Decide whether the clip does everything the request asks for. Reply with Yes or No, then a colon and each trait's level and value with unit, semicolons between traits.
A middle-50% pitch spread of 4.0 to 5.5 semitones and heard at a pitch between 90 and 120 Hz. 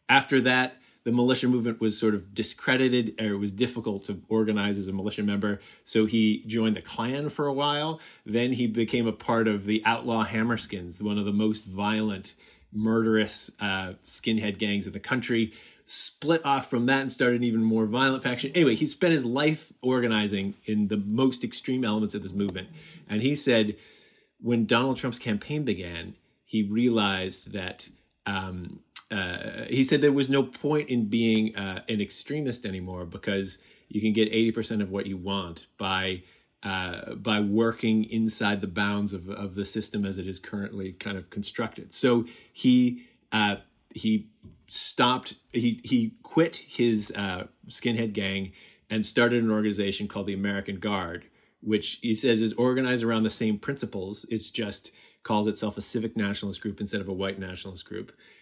No: average, 3.2 semitones; low, 110 Hz